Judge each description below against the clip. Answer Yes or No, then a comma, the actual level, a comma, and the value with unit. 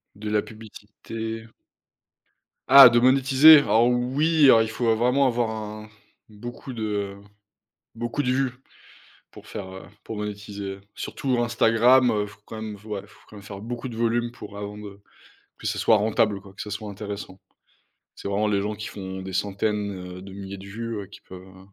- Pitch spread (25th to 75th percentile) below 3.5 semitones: Yes, average, 2.8 semitones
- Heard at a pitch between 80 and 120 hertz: Yes, low, 110 Hz